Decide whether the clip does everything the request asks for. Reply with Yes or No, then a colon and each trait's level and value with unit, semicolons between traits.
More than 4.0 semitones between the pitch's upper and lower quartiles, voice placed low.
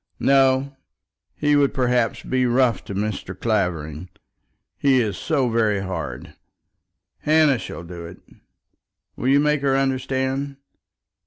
Yes: wide, 5.6 semitones; low, 125 Hz